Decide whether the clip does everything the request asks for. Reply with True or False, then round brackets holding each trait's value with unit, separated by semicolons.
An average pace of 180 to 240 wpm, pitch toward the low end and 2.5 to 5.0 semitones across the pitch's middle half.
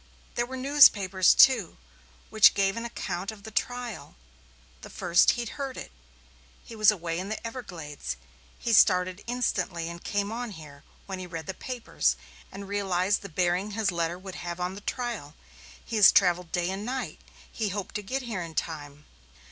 False (185 wpm; 195 Hz; 4.5 semitones)